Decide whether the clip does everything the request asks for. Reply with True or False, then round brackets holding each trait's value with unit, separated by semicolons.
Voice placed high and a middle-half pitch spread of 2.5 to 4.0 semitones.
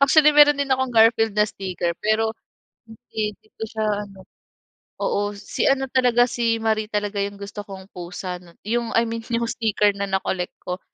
True (215 Hz; 2.8 semitones)